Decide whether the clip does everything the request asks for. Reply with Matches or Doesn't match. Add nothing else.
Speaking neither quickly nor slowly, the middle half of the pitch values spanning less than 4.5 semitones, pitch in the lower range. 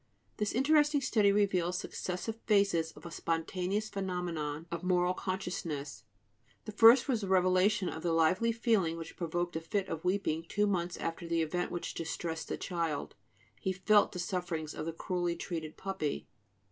Doesn't match